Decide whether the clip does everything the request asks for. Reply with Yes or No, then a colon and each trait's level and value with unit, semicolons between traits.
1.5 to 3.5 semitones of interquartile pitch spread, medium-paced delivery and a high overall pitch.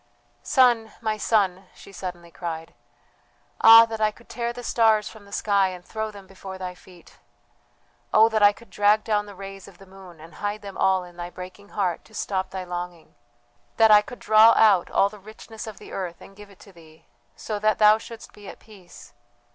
No: average, 2.8 semitones; fast, 210 wpm; high, 200 Hz